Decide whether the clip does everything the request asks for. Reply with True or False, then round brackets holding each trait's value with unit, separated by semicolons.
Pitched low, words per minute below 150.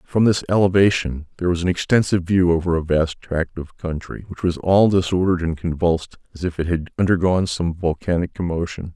False (85 Hz; 190 wpm)